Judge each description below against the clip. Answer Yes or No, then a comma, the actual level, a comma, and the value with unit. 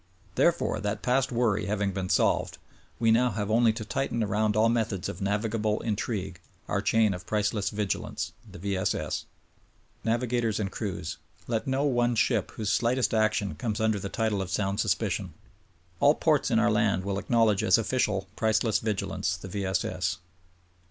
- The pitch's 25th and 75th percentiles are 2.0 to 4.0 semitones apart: Yes, narrow, 2.4 semitones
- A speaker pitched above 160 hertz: No, low, 110 Hz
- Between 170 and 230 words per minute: Yes, average, 175 wpm